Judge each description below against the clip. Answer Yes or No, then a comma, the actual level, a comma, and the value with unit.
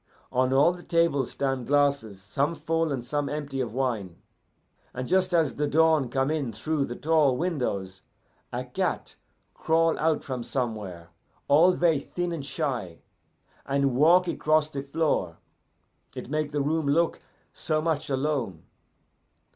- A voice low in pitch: No, medium, 145 Hz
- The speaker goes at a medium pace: Yes, average, 145 wpm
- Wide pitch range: No, average, 4.0 semitones